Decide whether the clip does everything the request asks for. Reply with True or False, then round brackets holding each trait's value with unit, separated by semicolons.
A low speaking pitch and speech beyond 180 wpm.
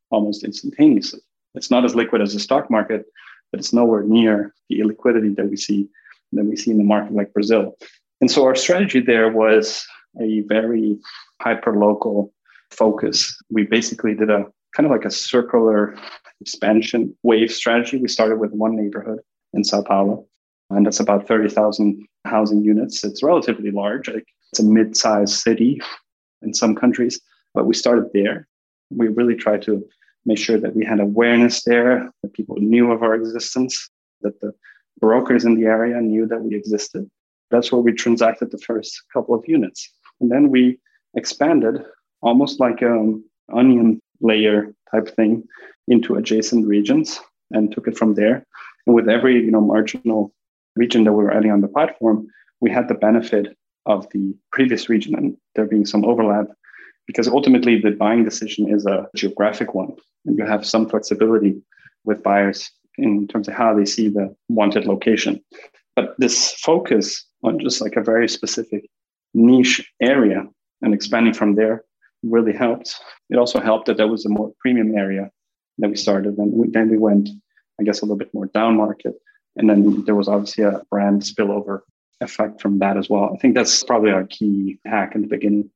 False (110 Hz; 175 wpm)